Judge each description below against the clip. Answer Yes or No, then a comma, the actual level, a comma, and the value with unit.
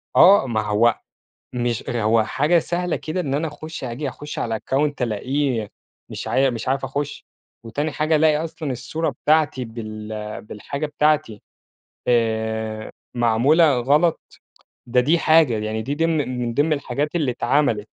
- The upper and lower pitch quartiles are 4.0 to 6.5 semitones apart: Yes, average, 4.9 semitones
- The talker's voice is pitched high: No, low, 135 Hz